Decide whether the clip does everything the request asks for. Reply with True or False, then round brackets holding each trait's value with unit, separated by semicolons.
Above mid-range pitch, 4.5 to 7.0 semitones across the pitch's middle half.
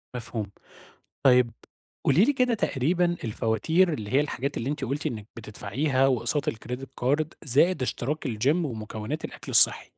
False (135 Hz; 5.1 semitones)